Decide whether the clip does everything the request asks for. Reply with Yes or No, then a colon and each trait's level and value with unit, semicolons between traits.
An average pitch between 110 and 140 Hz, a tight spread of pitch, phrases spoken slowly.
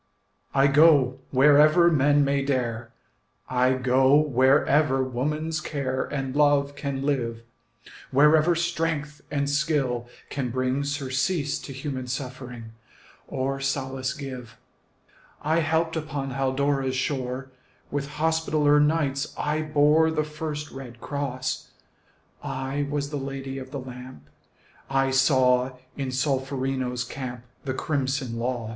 Yes: low, 135 Hz; narrow, 2.2 semitones; slow, 120 wpm